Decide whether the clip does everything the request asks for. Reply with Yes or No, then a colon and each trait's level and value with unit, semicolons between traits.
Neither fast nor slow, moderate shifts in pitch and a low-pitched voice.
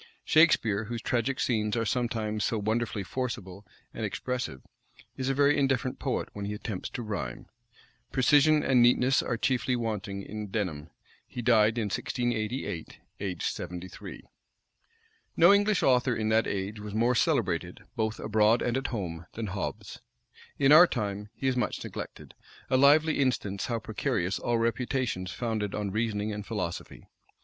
Yes: average, 155 wpm; average, 3.6 semitones; low, 110 Hz